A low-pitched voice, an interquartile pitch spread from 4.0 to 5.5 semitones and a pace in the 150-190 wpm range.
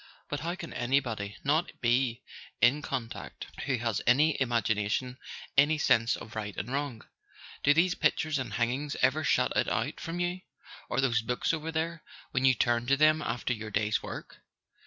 Yes: low, 130 Hz; average, 4.5 semitones; average, 175 wpm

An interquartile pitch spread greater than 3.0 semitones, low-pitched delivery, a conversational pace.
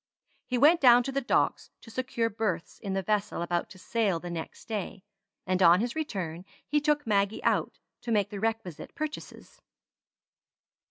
No: average, 5.1 semitones; high, 215 Hz; average, 170 wpm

